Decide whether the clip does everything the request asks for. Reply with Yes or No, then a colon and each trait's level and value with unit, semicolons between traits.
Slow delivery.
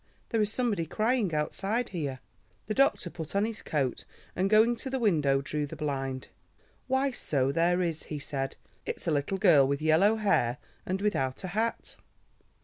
No: average, 175 wpm